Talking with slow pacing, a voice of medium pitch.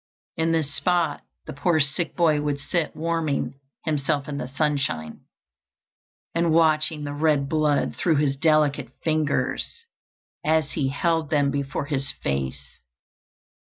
Yes: slow, 130 wpm; medium, 150 Hz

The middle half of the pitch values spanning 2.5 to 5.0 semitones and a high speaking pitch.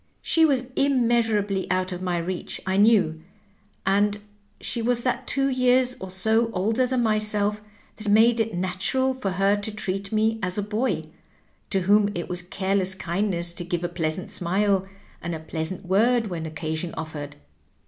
Yes: average, 3.8 semitones; high, 200 Hz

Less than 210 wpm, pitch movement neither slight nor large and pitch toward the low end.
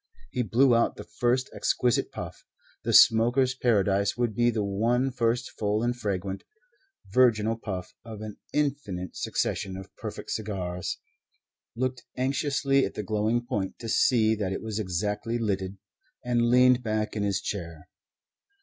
Yes: average, 150 wpm; average, 3.4 semitones; low, 110 Hz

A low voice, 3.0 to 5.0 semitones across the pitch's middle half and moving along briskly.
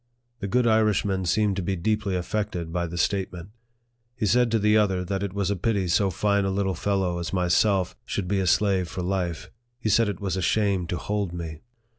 No: very low, 95 Hz; narrow, 2.6 semitones; fast, 215 wpm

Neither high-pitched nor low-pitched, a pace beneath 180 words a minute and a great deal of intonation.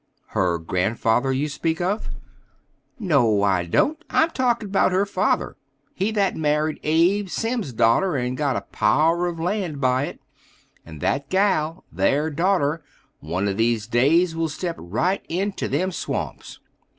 Yes: medium, 155 Hz; average, 150 wpm; wide, 7.4 semitones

